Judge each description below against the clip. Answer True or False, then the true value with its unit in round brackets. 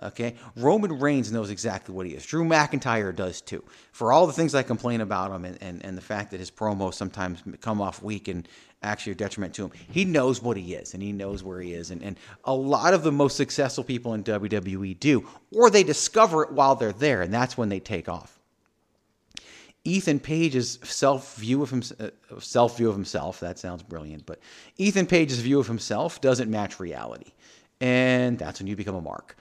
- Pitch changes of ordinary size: False (6.0 semitones)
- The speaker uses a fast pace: True (210 wpm)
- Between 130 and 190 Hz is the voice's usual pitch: False (110 Hz)